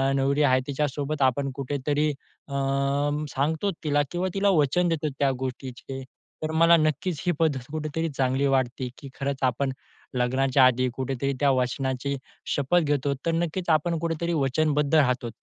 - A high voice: No, medium, 140 Hz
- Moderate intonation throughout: Yes, average, 3.0 semitones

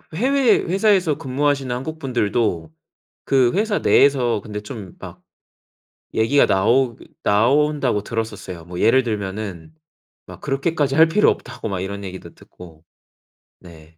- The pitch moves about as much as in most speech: No, wide, 6.5 semitones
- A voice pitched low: Yes, low, 120 Hz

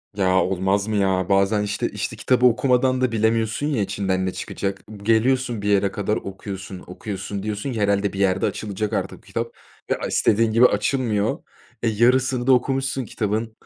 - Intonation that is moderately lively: Yes, average, 3.5 semitones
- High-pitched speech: No, low, 105 Hz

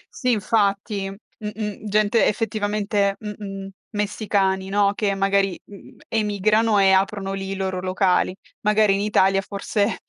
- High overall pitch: Yes, high, 200 Hz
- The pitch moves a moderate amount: No, narrow, 1.4 semitones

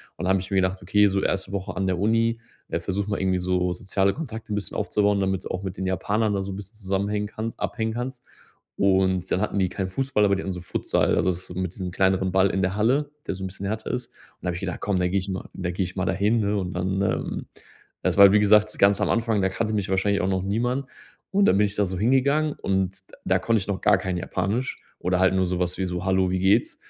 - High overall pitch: No, very low, 95 Hz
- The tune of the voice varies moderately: No, narrow, 2.1 semitones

